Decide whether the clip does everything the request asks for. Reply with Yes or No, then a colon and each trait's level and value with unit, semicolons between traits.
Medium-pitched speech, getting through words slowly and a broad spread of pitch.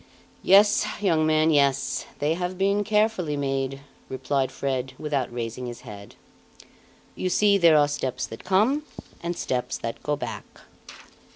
No: medium, 150 Hz; average, 145 wpm; wide, 6.0 semitones